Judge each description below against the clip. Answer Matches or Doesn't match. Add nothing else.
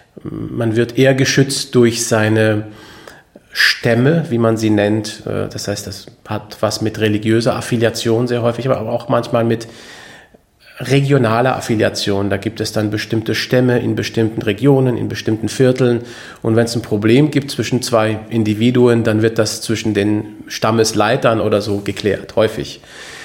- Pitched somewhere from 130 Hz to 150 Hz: Doesn't match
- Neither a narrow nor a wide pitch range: Doesn't match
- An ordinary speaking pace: Matches